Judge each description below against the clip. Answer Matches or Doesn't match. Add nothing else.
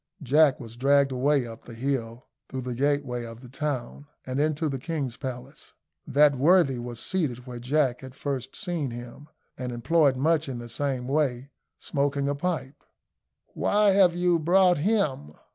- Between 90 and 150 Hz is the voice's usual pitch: Matches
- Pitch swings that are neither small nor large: Matches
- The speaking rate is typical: Matches